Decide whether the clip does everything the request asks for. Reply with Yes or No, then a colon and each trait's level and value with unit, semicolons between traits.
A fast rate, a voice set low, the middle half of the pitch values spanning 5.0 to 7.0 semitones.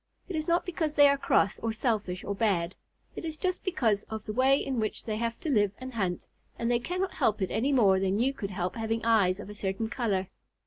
No: fast, 240 wpm; high, 225 Hz; average, 5.3 semitones